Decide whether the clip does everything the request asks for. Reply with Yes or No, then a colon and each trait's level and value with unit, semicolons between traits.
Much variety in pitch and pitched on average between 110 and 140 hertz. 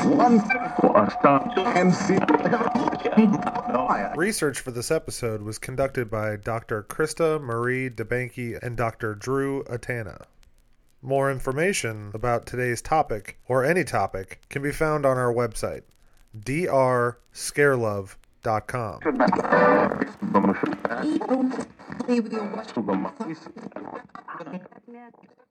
Yes: wide, 8.5 semitones; low, 135 Hz